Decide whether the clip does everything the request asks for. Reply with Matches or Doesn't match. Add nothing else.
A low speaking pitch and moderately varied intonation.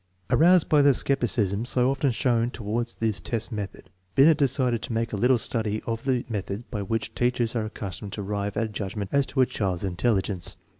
Matches